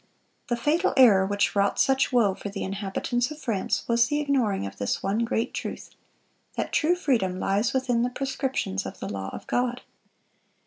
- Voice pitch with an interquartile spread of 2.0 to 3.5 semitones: No, average, 5.0 semitones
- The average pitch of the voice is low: No, high, 235 Hz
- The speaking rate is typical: Yes, average, 180 wpm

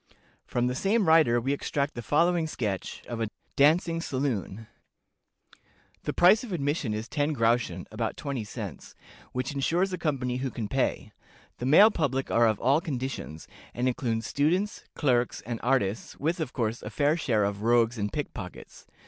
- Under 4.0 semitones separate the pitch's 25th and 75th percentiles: No, average, 5.2 semitones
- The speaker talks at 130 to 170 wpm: Yes, average, 165 wpm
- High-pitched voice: No, low, 130 Hz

